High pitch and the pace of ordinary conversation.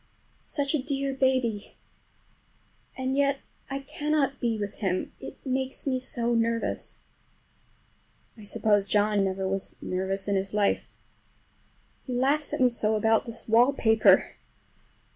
No: high, 230 Hz; slow, 130 wpm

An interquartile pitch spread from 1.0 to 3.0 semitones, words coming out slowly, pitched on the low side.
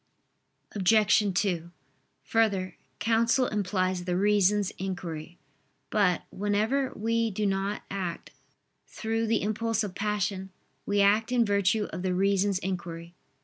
No: average, 2.7 semitones; slow, 120 wpm; high, 200 Hz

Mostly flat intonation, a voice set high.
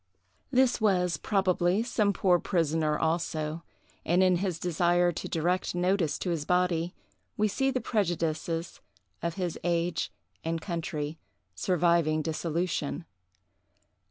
No: narrow, 2.1 semitones; medium, 175 Hz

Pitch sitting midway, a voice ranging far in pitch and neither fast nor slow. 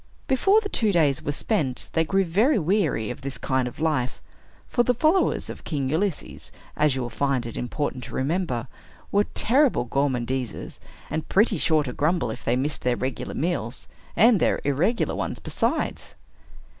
Yes: medium, 150 Hz; wide, 7.5 semitones; average, 170 wpm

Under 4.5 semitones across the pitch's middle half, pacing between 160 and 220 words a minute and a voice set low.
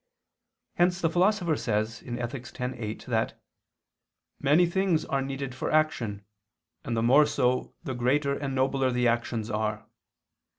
No: average, 4.1 semitones; average, 140 wpm; low, 130 Hz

